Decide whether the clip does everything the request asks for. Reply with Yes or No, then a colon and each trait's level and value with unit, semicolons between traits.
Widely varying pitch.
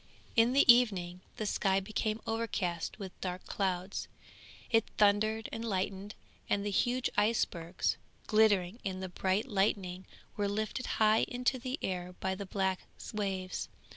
No: average, 2.9 semitones